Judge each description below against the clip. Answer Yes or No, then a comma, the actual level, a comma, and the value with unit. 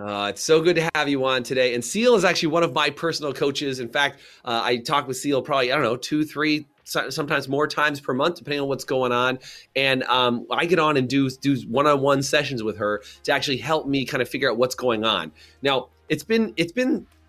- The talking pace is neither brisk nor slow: No, fast, 240 wpm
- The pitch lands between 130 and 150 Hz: Yes, medium, 140 Hz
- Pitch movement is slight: No, average, 3.5 semitones